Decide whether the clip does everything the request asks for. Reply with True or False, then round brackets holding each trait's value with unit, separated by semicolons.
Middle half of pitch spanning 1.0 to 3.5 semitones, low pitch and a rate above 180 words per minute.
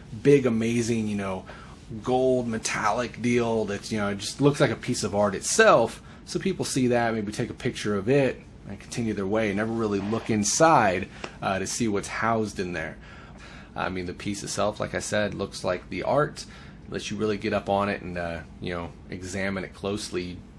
True (3.2 semitones; 105 Hz; 205 wpm)